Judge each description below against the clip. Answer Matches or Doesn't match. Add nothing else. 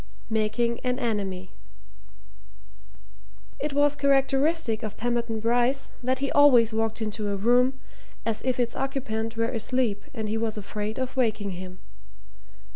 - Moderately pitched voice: Doesn't match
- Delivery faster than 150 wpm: Doesn't match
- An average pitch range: Matches